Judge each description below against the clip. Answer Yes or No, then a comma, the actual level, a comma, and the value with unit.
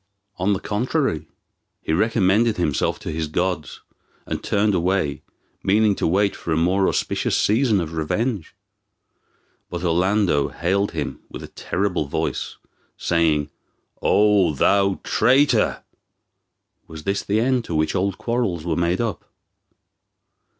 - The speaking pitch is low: Yes, very low, 95 Hz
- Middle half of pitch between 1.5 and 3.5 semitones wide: No, average, 4.1 semitones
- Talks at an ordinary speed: No, slow, 130 wpm